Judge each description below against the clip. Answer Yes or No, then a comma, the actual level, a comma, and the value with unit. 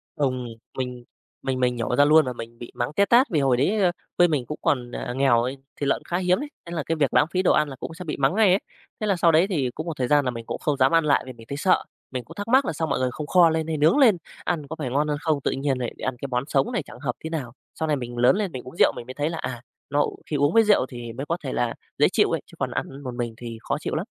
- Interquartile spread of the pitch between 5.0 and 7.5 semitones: No, average, 4.6 semitones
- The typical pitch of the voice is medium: Yes, medium, 145 Hz